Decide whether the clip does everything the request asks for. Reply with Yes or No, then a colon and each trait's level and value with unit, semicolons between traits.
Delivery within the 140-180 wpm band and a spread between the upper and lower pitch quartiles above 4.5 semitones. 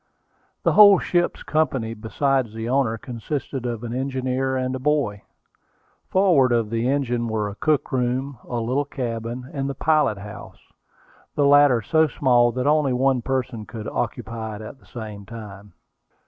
No: average, 160 wpm; average, 3.4 semitones